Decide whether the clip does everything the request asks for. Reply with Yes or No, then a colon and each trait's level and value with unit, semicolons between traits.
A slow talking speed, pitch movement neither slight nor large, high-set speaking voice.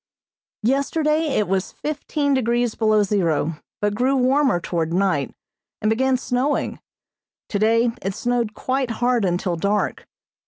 Yes: slow, 125 wpm; average, 4.9 semitones; high, 230 Hz